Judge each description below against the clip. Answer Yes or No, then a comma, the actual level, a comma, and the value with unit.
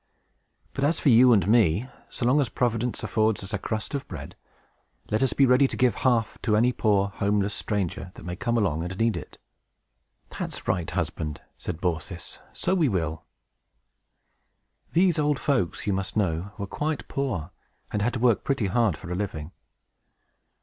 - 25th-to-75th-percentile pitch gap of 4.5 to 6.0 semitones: Yes, average, 5.0 semitones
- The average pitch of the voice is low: Yes, low, 105 Hz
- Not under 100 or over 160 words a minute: No, average, 175 wpm